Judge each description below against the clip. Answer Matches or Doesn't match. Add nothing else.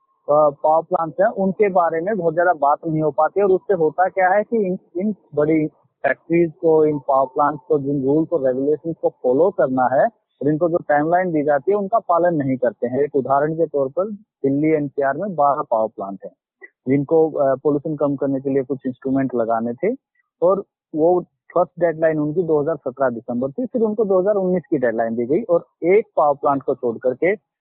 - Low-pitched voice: Doesn't match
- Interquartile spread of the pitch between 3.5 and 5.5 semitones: Matches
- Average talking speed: Doesn't match